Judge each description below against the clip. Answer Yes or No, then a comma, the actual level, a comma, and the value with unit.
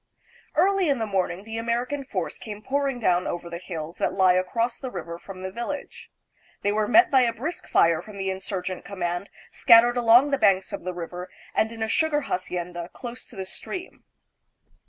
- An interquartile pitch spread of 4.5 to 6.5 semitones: Yes, average, 5.1 semitones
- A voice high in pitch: Yes, high, 210 Hz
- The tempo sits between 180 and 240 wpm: Yes, average, 200 wpm